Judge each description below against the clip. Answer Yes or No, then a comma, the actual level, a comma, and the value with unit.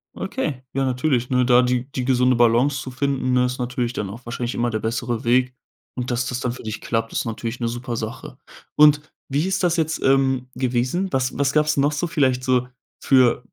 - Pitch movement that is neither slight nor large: No, narrow, 2.1 semitones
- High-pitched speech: No, low, 125 Hz